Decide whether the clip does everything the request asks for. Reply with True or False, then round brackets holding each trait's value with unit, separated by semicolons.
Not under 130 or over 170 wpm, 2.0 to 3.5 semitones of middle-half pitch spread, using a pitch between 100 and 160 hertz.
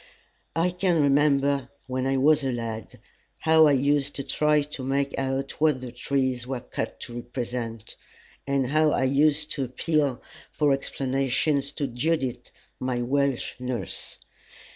True (145 wpm; 2.5 semitones; 135 Hz)